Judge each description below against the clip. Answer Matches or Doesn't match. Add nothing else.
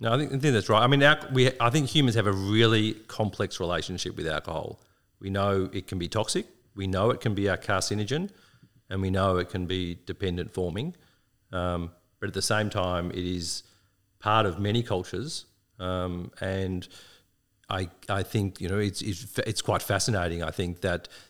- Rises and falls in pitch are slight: Doesn't match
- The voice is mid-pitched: Doesn't match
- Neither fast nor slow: Matches